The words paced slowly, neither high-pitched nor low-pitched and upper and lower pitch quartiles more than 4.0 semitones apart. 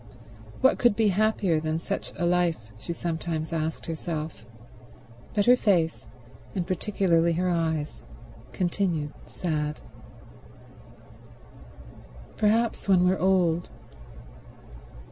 No: slow, 100 wpm; medium, 175 Hz; average, 3.0 semitones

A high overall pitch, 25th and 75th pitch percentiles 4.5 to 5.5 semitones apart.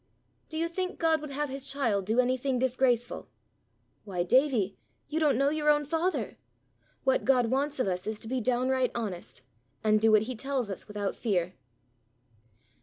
Yes: very high, 255 Hz; average, 4.9 semitones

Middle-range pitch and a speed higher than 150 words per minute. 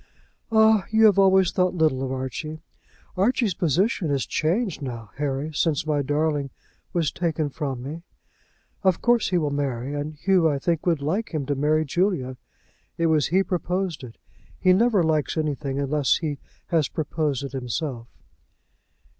Yes: medium, 155 Hz; average, 160 wpm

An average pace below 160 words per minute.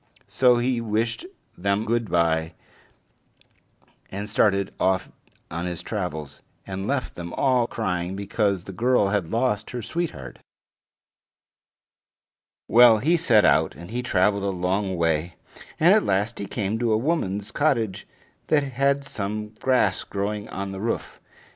Yes: average, 140 wpm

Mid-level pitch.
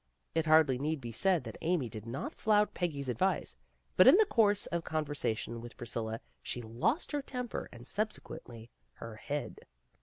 Yes: medium, 145 Hz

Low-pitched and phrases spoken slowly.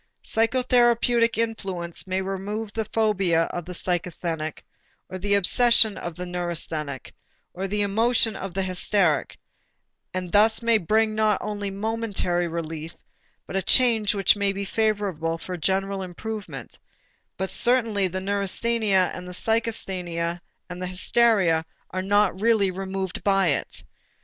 No: high, 195 Hz; slow, 130 wpm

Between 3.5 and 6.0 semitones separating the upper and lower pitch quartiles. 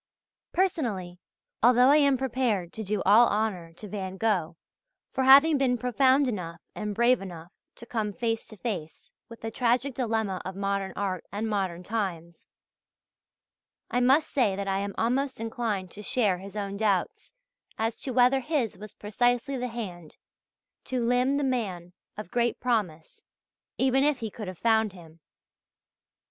Yes: average, 4.4 semitones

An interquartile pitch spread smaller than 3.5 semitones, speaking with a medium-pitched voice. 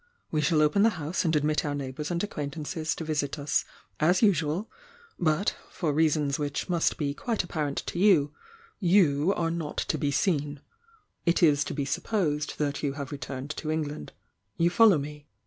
Yes: average, 2.9 semitones; medium, 155 Hz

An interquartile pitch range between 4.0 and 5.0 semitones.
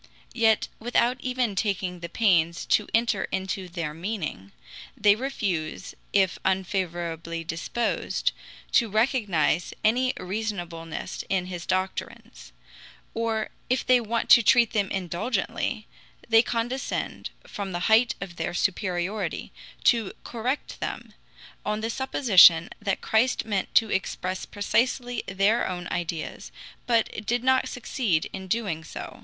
Yes: average, 4.6 semitones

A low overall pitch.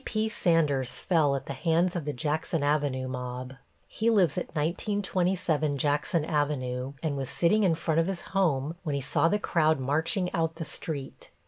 No: medium, 155 Hz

